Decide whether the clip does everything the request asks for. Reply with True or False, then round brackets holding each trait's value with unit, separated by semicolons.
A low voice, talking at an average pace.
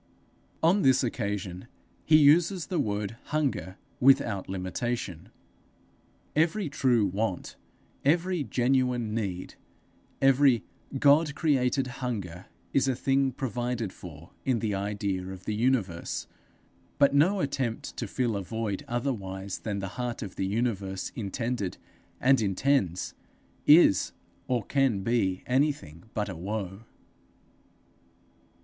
False (115 Hz; 120 wpm)